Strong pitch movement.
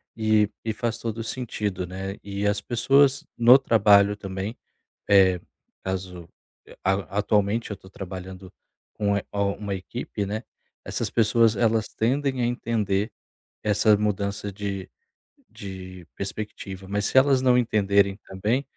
No: average, 2.8 semitones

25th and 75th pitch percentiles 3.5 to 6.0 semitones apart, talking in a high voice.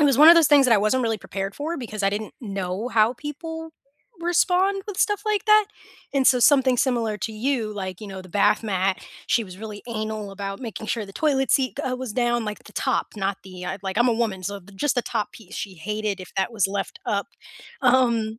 Yes: average, 4.9 semitones; high, 220 Hz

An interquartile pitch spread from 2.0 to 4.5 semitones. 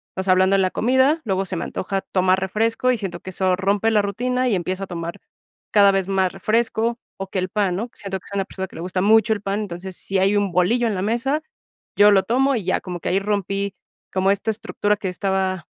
Yes: narrow, 2.6 semitones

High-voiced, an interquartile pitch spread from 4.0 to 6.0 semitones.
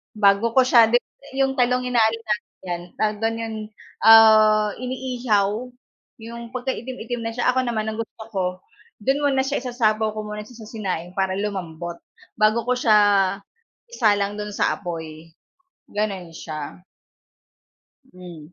No: high, 215 Hz; average, 3.5 semitones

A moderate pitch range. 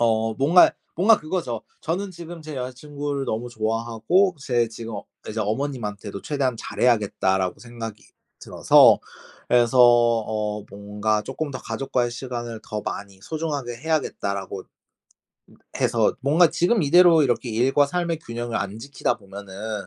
Yes: average, 5.0 semitones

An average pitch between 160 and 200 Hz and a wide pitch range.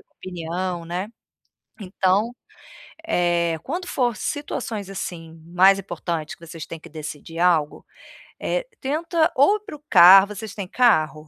Yes: medium, 185 Hz; wide, 6.1 semitones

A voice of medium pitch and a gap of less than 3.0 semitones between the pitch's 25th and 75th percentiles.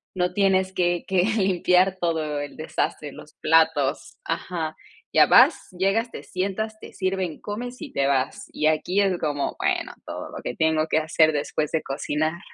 No: medium, 175 Hz; average, 3.5 semitones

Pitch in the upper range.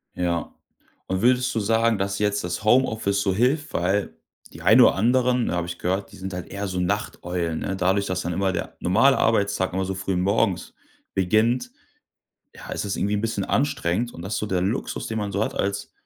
No: low, 100 Hz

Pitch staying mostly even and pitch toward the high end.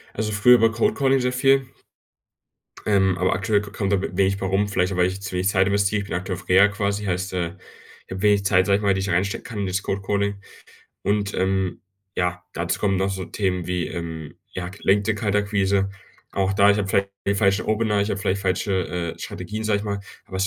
No: narrow, 1.8 semitones; low, 100 Hz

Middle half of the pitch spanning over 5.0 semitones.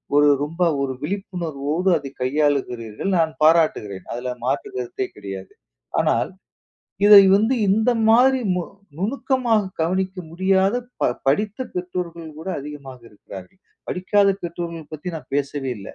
Yes: wide, 5.6 semitones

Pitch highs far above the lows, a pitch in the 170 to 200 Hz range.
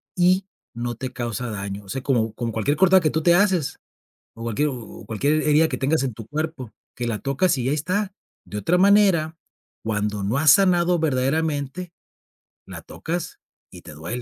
No: wide, 6.7 semitones; medium, 140 Hz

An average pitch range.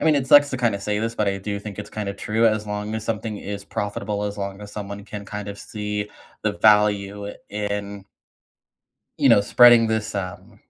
No: narrow, 1.1 semitones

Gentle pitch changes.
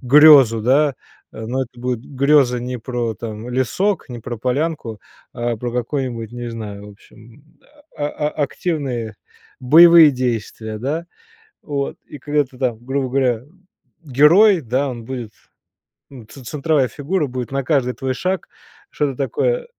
No: average, 3.6 semitones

